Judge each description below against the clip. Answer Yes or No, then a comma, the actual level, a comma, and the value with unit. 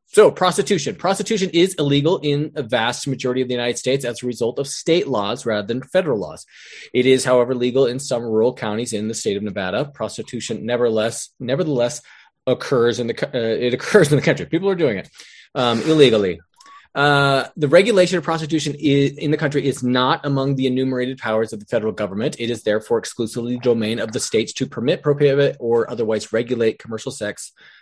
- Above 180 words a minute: Yes, average, 195 wpm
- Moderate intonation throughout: Yes, average, 4.0 semitones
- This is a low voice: Yes, low, 130 Hz